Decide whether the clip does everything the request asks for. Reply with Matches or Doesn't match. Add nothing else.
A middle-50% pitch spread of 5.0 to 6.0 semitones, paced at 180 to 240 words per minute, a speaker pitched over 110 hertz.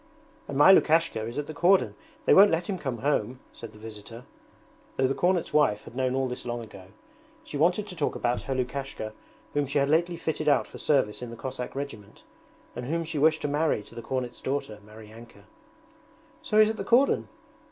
Matches